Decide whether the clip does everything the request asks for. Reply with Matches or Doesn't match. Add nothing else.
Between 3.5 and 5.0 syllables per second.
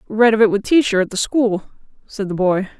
Doesn't match